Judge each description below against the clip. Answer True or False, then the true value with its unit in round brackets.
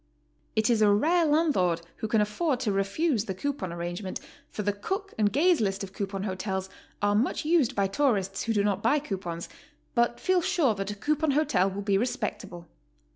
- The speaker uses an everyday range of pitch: False (6.7 semitones)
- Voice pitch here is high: True (210 Hz)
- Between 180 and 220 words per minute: True (190 wpm)